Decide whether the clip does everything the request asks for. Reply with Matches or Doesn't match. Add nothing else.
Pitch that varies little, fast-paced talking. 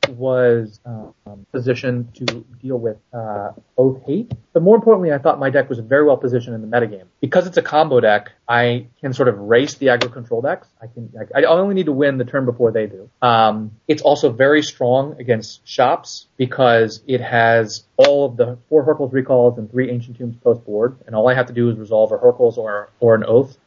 Doesn't match